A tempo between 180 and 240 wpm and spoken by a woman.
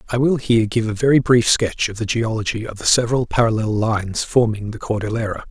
No: fast, 205 wpm; male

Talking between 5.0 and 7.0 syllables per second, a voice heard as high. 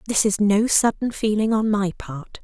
No: 4.6 syllables/s; high, 210 Hz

